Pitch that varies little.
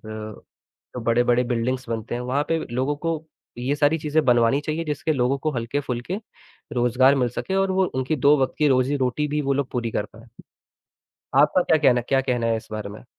No: average, 3.4 semitones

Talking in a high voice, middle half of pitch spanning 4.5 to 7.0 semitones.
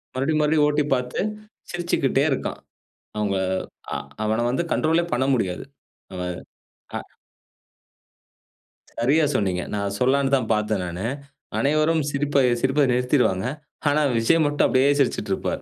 No: low, 135 Hz; average, 5.1 semitones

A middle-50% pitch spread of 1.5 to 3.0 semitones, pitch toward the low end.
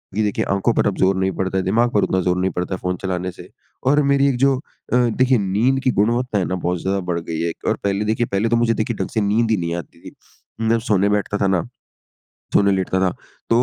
No: average, 3.7 semitones; low, 100 Hz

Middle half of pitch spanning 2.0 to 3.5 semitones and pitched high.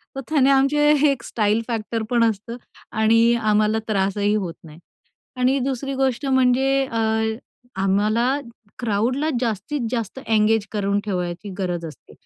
No: average, 4.0 semitones; high, 225 Hz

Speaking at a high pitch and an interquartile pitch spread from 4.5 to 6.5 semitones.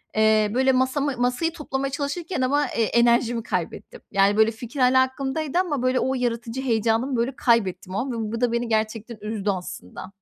No: high, 240 Hz; average, 3.3 semitones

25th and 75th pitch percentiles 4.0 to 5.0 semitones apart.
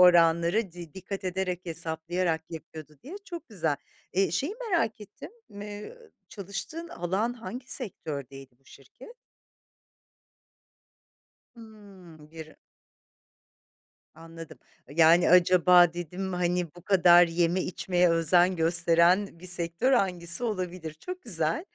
No: average, 3.2 semitones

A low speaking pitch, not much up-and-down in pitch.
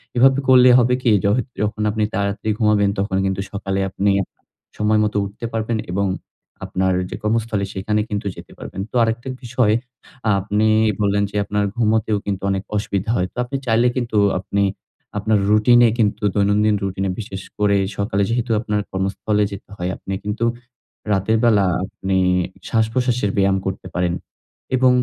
Yes: low, 105 Hz; narrow, 2.2 semitones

